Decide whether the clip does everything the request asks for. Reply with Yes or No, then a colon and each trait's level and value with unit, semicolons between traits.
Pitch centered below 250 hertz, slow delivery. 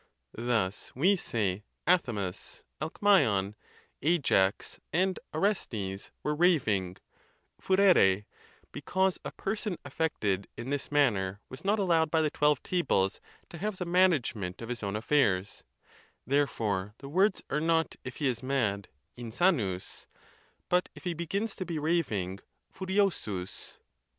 Yes: medium, 140 Hz; slow, 130 wpm